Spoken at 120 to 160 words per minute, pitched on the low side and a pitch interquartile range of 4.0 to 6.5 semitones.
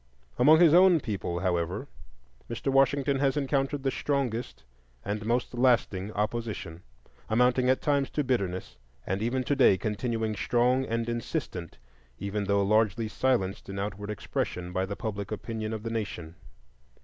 Yes: average, 145 wpm; low, 115 Hz; average, 4.7 semitones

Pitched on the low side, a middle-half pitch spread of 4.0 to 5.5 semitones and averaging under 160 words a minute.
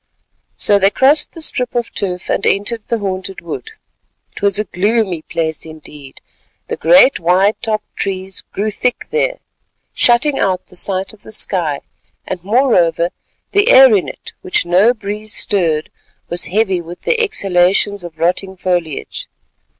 No: high, 195 Hz; average, 4.4 semitones; average, 150 wpm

